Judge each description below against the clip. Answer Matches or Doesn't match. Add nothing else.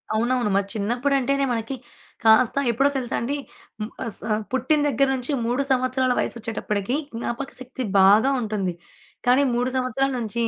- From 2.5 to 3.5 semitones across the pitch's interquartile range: Matches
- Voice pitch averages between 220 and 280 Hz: Matches